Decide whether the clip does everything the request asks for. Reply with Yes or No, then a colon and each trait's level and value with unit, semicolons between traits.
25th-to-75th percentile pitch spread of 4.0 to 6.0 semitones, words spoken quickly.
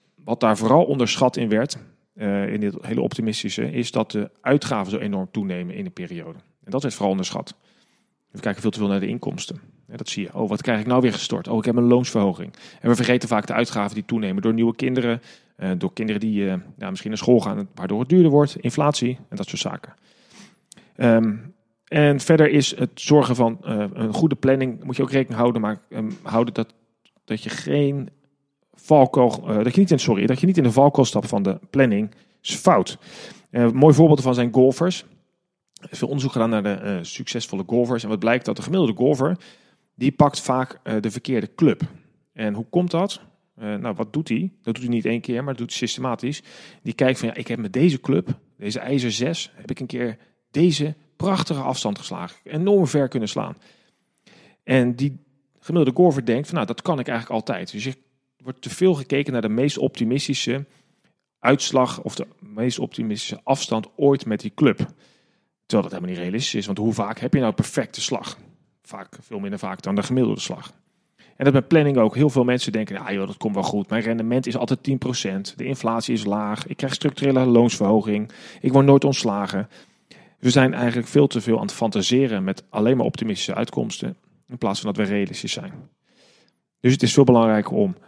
Yes: average, 4.4 semitones; fast, 210 wpm